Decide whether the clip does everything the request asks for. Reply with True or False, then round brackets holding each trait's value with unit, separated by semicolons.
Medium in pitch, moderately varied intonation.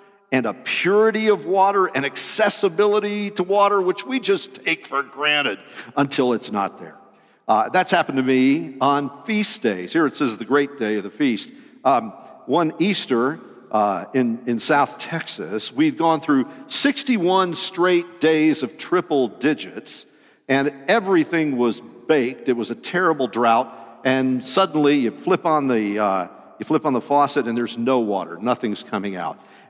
False (145 Hz; 7.5 semitones)